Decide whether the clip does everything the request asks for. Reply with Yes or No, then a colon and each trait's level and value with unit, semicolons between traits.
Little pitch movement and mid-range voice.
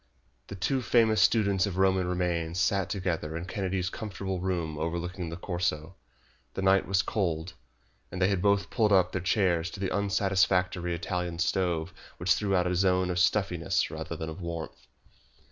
No: narrow, 2.0 semitones; very low, 90 Hz